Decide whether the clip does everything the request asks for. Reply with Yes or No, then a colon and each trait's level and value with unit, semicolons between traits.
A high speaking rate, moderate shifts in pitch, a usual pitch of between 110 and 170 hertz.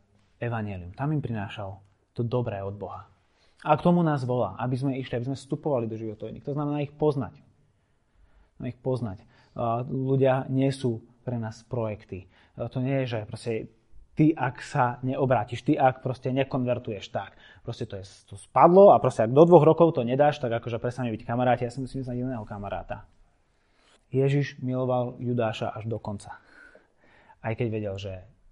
Yes: fast, 180 wpm; average, 3.4 semitones; low, 120 Hz